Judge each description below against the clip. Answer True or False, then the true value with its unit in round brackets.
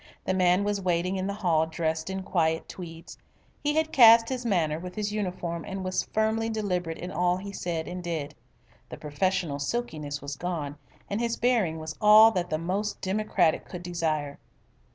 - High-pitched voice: False (180 Hz)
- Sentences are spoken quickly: False (180 wpm)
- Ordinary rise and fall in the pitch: True (4.2 semitones)